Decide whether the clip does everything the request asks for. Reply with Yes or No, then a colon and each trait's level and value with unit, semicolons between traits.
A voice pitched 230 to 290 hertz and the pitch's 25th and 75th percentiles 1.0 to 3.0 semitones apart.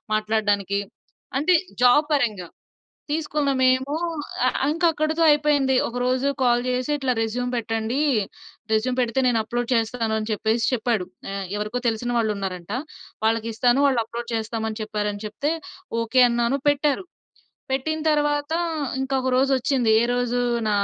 No: high, 245 Hz; average, 3.5 semitones